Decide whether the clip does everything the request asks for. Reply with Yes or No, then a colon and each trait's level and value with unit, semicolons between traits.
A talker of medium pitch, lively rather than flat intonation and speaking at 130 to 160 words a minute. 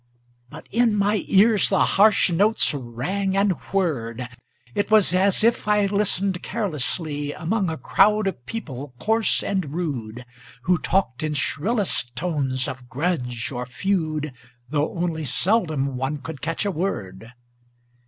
Yes: medium, 165 Hz; wide, 6.9 semitones; average, 140 wpm